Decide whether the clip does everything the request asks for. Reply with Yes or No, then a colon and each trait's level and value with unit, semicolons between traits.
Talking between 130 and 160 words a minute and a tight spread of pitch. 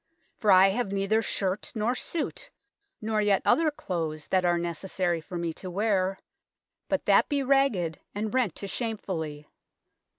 No: average, 155 wpm; average, 4.2 semitones